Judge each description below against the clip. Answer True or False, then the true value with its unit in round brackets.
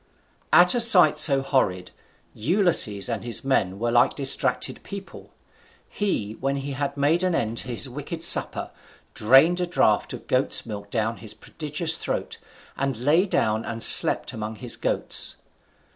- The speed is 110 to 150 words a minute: False (160 wpm)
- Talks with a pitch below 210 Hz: True (135 Hz)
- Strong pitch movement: True (6.3 semitones)